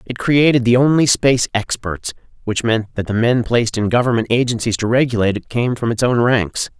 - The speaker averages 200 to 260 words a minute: Yes, fast, 205 wpm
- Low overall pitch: Yes, low, 115 Hz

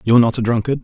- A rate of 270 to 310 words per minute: Yes, fast, 290 wpm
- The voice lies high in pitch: No, low, 115 Hz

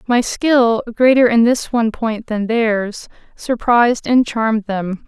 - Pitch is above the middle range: Yes, high, 230 Hz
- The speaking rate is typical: Yes, average, 155 wpm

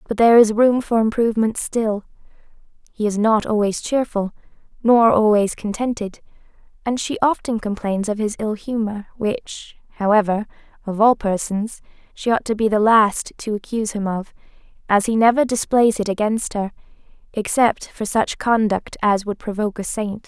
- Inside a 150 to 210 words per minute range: Yes, average, 160 wpm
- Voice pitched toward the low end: No, high, 215 Hz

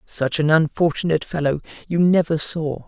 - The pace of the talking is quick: No, average, 145 wpm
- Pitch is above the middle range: No, medium, 160 Hz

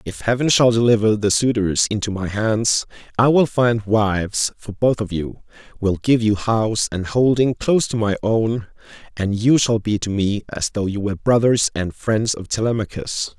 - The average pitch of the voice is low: Yes, low, 110 Hz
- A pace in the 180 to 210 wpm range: Yes, average, 190 wpm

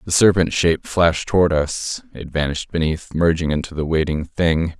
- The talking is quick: No, average, 175 wpm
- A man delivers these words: Yes, male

